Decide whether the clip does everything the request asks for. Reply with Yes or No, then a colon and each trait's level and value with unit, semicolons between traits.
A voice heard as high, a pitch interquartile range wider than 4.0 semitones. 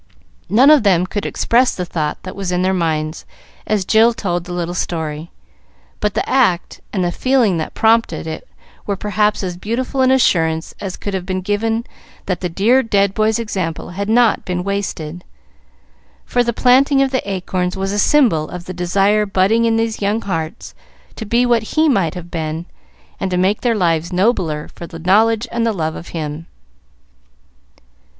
Yes: high, 195 Hz; average, 4.4 semitones